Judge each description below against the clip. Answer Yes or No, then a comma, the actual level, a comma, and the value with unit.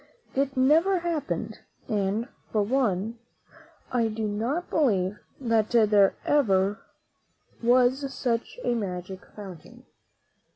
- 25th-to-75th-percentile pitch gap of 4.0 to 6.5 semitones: Yes, average, 4.7 semitones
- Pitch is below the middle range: No, high, 230 Hz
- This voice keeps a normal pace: No, slow, 100 wpm